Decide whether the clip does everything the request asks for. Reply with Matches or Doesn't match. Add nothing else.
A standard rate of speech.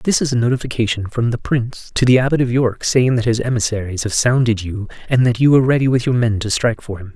Doesn't match